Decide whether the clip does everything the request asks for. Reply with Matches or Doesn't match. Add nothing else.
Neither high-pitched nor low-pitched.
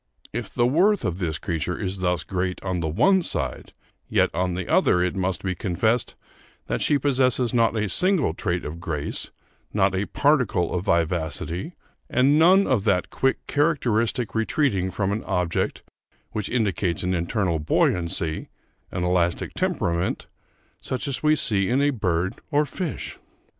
Doesn't match